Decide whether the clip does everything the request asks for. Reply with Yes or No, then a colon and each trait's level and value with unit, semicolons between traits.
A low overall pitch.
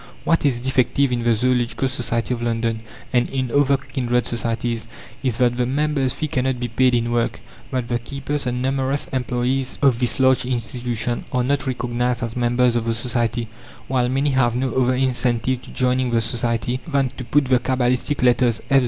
Yes: low, 125 Hz